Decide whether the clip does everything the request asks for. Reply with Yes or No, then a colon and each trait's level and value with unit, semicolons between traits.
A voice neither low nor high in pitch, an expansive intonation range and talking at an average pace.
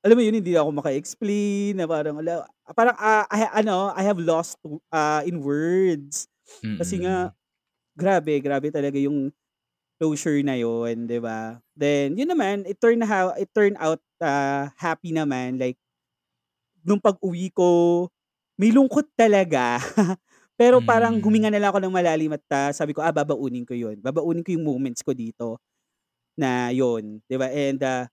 No: medium, 160 Hz; wide, 6.1 semitones; fast, 165 wpm